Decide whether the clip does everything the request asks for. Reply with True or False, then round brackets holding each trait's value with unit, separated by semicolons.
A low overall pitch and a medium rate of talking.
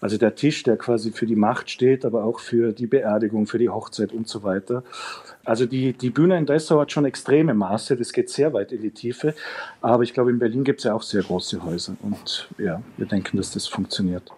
False (120 Hz; 235 wpm)